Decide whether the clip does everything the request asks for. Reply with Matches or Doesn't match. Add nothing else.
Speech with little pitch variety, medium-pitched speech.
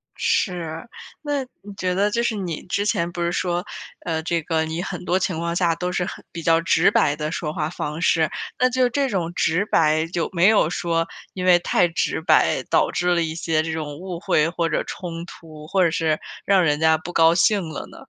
Matches